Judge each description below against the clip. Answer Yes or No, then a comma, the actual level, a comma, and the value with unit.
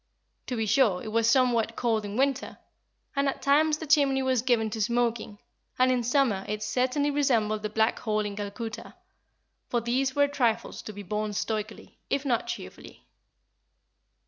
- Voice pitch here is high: Yes, high, 235 Hz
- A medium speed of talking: Yes, average, 170 wpm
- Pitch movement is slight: No, average, 3.8 semitones